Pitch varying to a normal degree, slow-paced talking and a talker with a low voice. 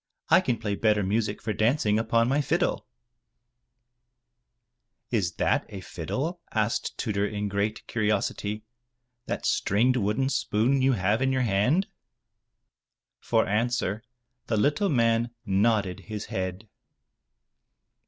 Yes: average, 3.2 semitones; slow, 125 wpm; low, 110 Hz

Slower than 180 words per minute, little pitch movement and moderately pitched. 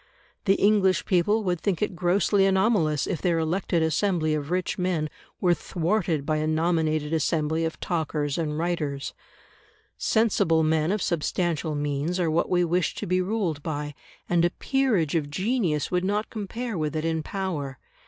No: average, 165 wpm; average, 3.4 semitones; medium, 170 Hz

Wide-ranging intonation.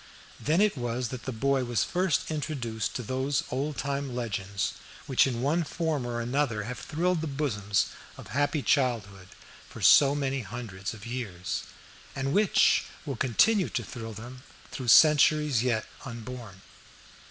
No: average, 4.1 semitones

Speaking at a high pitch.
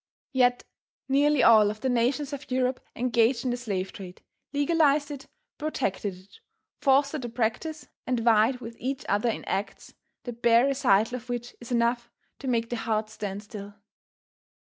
Yes: high, 240 Hz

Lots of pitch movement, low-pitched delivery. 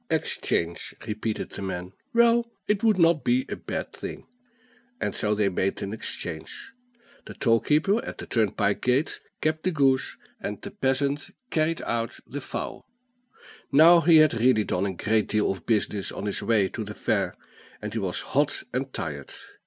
Yes: wide, 7.2 semitones; low, 120 Hz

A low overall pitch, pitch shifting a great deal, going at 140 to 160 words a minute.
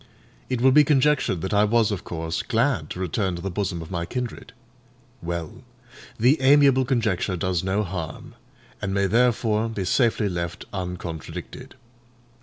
Yes: low, 100 Hz; wide, 5.7 semitones; average, 155 wpm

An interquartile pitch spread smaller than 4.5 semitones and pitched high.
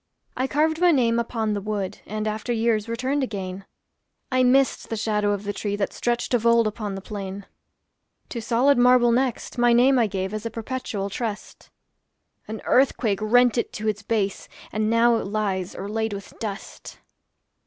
Yes: average, 2.8 semitones; high, 220 Hz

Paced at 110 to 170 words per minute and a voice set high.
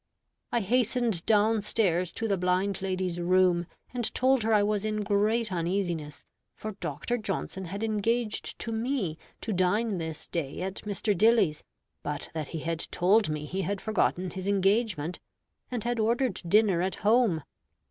Yes: average, 160 wpm; high, 200 Hz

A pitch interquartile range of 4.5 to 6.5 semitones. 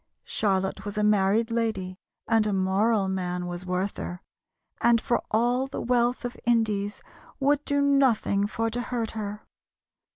No: average, 3.6 semitones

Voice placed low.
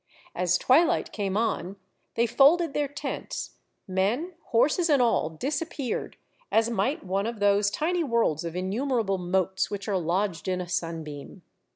No: high, 205 Hz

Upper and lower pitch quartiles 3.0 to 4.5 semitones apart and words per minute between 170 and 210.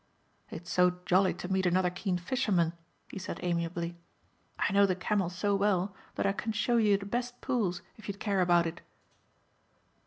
No: narrow, 2.5 semitones; average, 180 wpm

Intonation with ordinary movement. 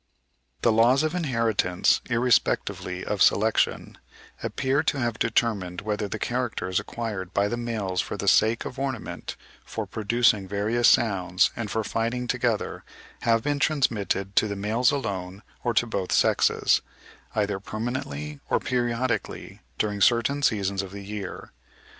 Yes: average, 3.2 semitones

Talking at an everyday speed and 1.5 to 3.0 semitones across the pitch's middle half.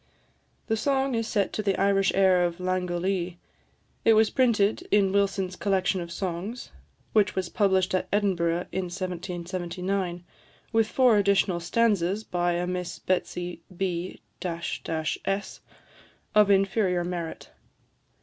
No: slow, 125 wpm; narrow, 2.4 semitones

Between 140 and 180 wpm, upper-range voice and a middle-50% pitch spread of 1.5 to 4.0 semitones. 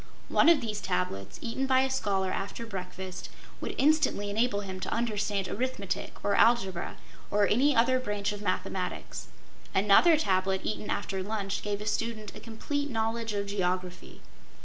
Yes: average, 155 wpm; high, 210 Hz; average, 3.4 semitones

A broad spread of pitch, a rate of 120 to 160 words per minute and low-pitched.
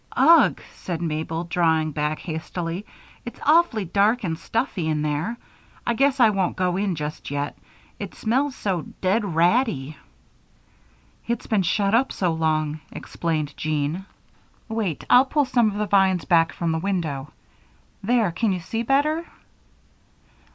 No: wide, 5.9 semitones; average, 145 wpm; medium, 185 Hz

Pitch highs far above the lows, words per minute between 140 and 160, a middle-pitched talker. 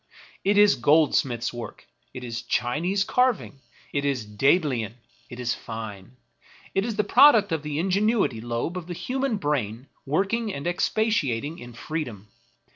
Yes: wide, 8.6 semitones; average, 150 wpm; medium, 150 Hz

